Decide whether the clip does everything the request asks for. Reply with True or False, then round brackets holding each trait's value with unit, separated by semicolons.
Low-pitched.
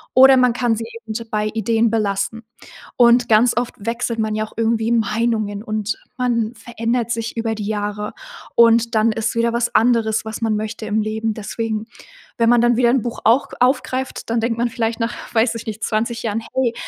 False (230 Hz)